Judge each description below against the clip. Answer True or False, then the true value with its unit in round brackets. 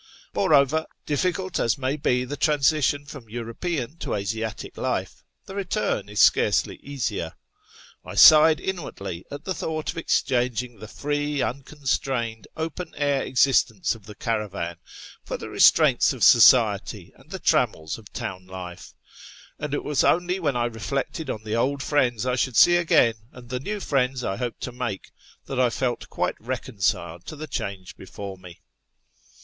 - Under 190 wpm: True (160 wpm)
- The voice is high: False (125 Hz)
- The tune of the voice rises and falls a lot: False (5.0 semitones)